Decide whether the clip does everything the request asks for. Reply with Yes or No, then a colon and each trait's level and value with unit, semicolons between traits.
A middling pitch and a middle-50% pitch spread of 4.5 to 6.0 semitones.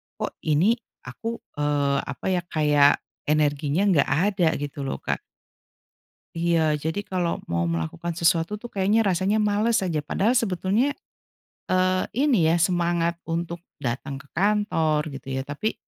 Yes: medium, 170 Hz; average, 5.2 semitones